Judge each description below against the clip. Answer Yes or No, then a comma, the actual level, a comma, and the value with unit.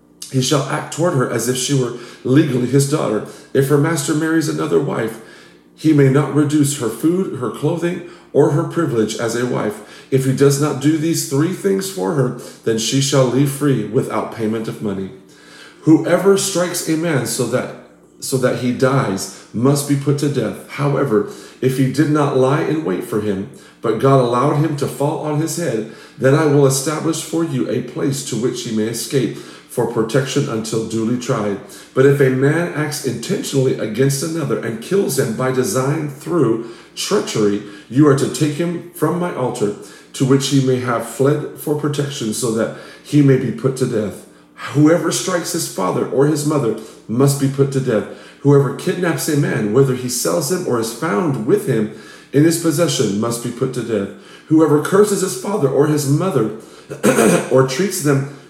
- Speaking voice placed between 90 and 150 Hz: Yes, medium, 140 Hz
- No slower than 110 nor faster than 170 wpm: No, average, 190 wpm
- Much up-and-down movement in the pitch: No, average, 3.9 semitones